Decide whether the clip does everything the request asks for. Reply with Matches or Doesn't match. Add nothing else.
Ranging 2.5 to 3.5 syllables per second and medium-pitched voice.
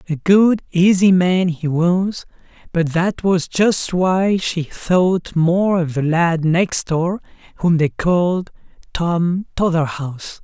Matches